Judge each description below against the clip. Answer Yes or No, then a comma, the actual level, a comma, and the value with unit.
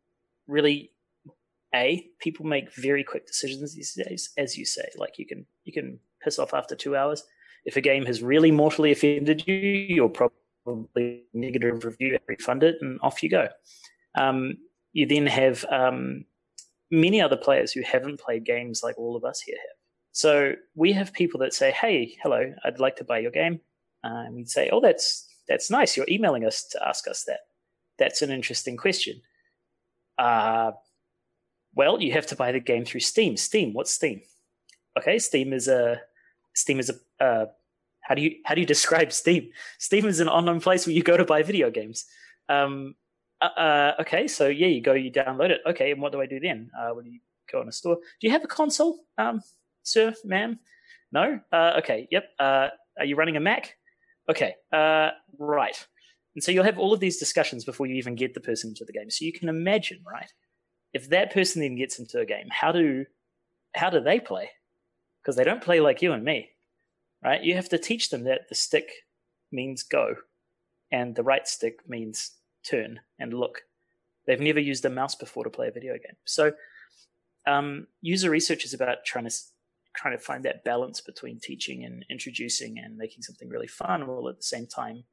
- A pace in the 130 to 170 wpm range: No, average, 195 wpm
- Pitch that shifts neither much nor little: No, wide, 7.0 semitones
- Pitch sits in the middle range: Yes, medium, 155 Hz